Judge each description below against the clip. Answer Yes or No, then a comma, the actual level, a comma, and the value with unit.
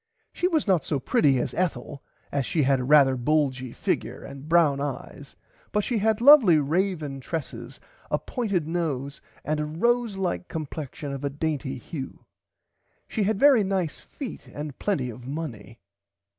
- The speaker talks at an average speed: Yes, average, 160 wpm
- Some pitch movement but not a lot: No, wide, 5.8 semitones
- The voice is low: No, medium, 155 Hz